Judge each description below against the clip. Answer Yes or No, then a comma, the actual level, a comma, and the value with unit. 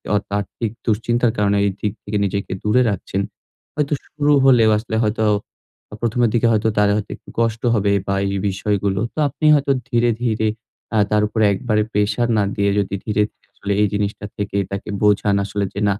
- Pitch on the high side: No, low, 105 Hz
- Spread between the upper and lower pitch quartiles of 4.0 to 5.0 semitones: No, narrow, 2.4 semitones